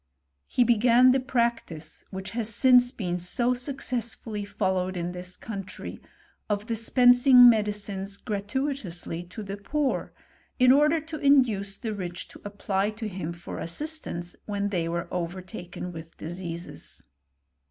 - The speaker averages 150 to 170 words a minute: No, slow, 135 wpm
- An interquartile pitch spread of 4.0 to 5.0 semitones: No, wide, 5.4 semitones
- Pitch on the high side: Yes, high, 205 Hz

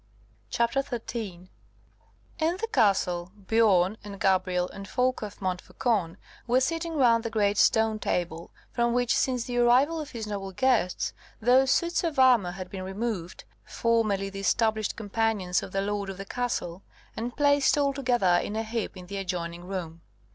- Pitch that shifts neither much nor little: Yes, average, 4.6 semitones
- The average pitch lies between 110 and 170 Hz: No, high, 215 Hz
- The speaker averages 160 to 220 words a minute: Yes, average, 165 wpm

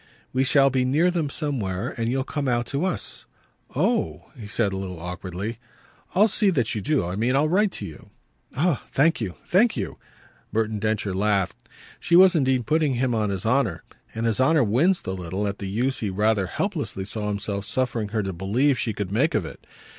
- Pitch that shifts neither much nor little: No, wide, 5.9 semitones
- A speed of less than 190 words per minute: No, fast, 205 wpm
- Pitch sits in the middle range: No, low, 115 Hz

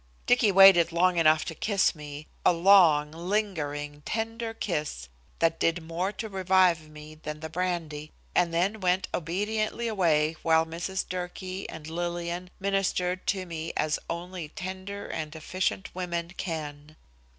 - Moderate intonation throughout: Yes, average, 3.1 semitones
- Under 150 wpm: Yes, average, 140 wpm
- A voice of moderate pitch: Yes, medium, 175 Hz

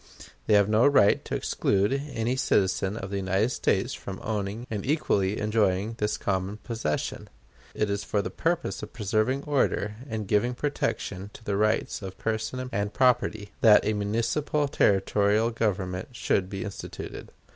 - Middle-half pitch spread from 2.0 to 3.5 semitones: Yes, average, 2.7 semitones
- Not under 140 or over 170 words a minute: Yes, average, 155 wpm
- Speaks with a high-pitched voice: No, low, 105 Hz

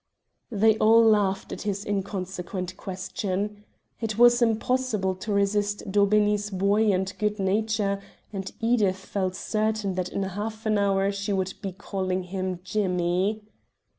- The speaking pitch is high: Yes, high, 200 Hz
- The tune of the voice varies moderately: No, narrow, 2.1 semitones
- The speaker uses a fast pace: No, slow, 135 wpm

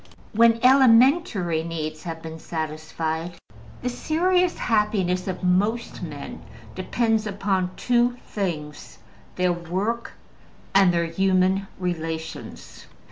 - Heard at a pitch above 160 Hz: Yes, medium, 185 Hz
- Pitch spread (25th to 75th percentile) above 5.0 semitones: Yes, wide, 5.5 semitones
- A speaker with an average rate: No, slow, 100 wpm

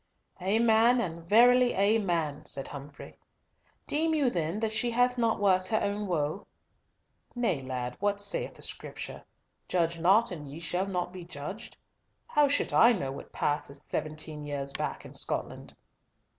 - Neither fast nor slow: Yes, average, 155 wpm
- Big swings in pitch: Yes, wide, 6.7 semitones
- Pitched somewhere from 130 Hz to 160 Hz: No, medium, 185 Hz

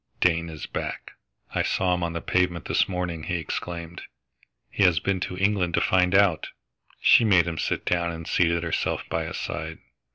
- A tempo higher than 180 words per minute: Yes, average, 190 wpm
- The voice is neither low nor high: No, very low, 85 Hz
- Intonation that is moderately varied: No, narrow, 1.6 semitones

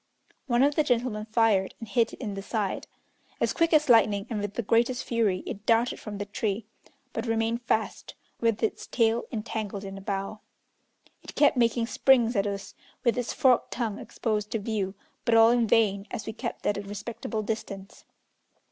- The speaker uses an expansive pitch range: No, narrow, 2.5 semitones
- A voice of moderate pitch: No, high, 225 Hz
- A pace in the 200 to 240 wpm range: No, average, 190 wpm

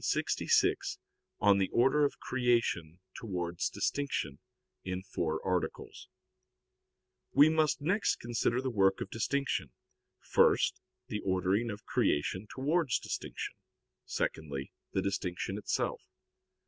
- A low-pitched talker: Yes, low, 105 Hz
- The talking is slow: Yes, slow, 115 wpm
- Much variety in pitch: Yes, wide, 6.3 semitones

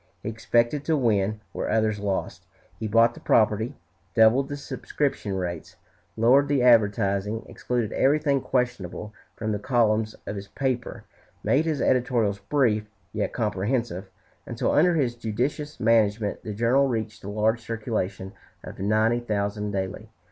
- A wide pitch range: No, average, 3.2 semitones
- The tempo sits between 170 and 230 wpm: No, average, 140 wpm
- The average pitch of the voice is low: Yes, low, 110 Hz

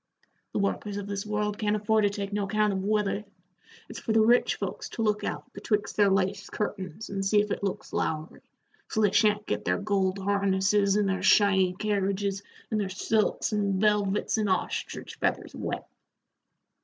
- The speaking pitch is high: Yes, high, 205 Hz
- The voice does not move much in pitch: Yes, narrow, 1.3 semitones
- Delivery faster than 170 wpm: Yes, average, 180 wpm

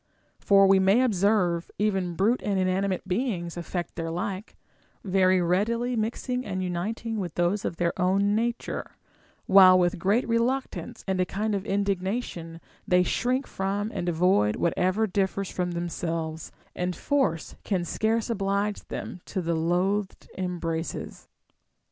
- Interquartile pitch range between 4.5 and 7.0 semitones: No, average, 3.1 semitones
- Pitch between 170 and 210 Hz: Yes, high, 190 Hz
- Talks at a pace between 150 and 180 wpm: No, average, 140 wpm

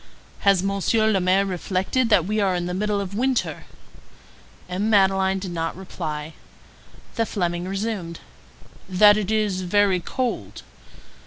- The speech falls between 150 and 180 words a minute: No, average, 140 wpm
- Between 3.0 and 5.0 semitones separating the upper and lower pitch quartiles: No, narrow, 2.6 semitones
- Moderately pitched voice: No, high, 195 Hz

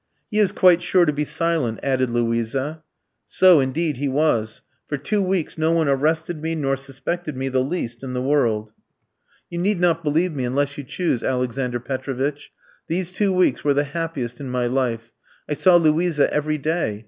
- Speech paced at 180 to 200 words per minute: Yes, average, 185 wpm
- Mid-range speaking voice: Yes, medium, 145 Hz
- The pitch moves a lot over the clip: No, average, 4.4 semitones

